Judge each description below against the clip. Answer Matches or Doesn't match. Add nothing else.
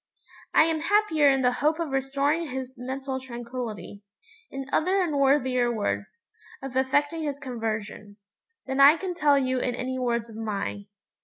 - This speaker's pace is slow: Doesn't match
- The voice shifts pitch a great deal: Doesn't match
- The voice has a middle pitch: Doesn't match